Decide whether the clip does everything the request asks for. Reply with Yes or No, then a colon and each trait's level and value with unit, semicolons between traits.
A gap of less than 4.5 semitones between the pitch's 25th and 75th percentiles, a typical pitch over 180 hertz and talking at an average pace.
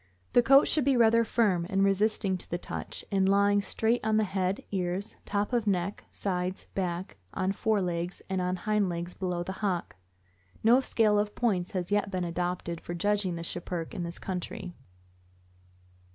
Yes: average, 2.8 semitones; high, 190 Hz; average, 175 wpm